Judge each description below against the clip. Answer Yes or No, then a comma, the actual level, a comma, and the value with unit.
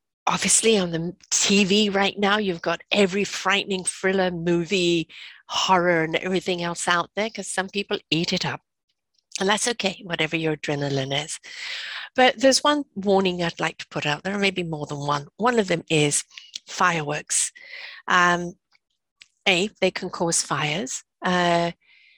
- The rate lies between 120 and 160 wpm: Yes, average, 155 wpm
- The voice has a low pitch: No, medium, 185 Hz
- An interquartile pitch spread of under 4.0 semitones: Yes, average, 3.3 semitones